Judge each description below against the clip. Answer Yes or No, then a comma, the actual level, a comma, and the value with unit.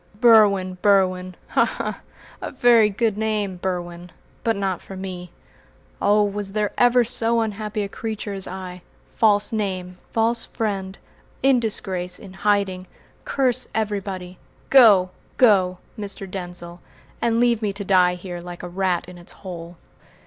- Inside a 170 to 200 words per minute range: No, average, 145 wpm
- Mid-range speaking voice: No, high, 195 Hz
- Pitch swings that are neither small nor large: Yes, average, 3.0 semitones